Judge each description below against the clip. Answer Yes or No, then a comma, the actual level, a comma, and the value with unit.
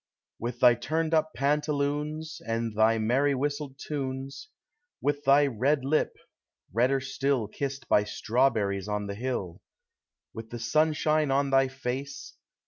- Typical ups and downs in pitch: Yes, average, 3.8 semitones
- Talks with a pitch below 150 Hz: Yes, low, 135 Hz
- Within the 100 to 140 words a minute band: Yes, slow, 135 wpm